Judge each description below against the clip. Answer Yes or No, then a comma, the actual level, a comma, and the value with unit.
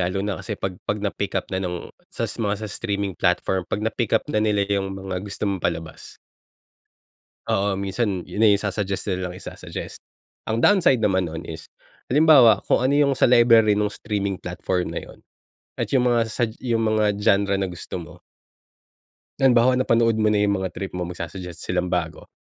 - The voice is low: Yes, low, 100 Hz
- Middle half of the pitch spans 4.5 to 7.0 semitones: No, average, 3.2 semitones